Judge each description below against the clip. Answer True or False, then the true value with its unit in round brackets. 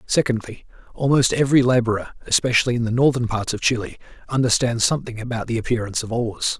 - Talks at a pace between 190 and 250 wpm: False (165 wpm)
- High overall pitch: False (120 Hz)